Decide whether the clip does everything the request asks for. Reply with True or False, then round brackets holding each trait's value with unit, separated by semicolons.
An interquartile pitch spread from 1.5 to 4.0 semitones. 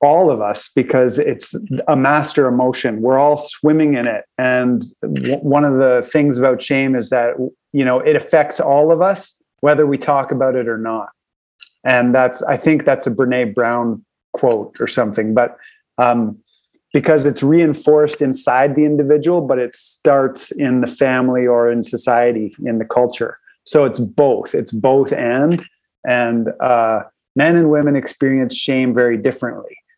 True (3.3 semitones)